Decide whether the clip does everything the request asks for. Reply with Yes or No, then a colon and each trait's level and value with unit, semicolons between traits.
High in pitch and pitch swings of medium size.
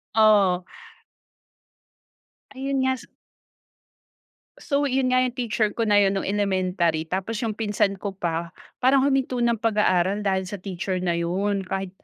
Yes: high, 205 Hz; average, 4.2 semitones